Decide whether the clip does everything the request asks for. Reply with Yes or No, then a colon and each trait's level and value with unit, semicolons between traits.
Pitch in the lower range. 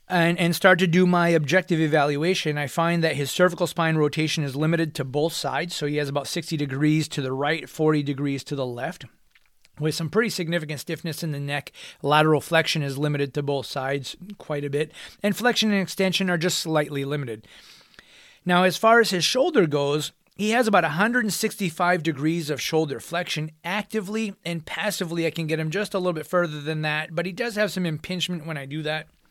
No: medium, 165 Hz